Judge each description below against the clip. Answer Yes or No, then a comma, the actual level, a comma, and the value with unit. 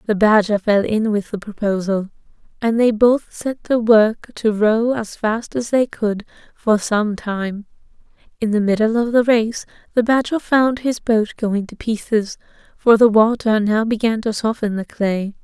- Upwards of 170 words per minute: Yes, average, 180 wpm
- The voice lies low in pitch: No, high, 220 Hz